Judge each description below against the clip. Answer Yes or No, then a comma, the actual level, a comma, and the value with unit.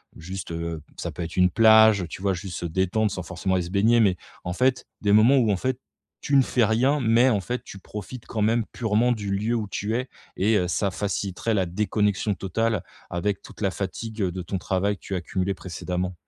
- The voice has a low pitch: Yes, low, 100 Hz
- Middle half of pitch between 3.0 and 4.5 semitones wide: Yes, average, 3.5 semitones